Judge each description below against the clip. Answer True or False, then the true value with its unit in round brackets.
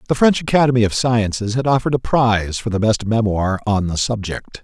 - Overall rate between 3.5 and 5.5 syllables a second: False (5.9 syllables/s)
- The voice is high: False (115 Hz)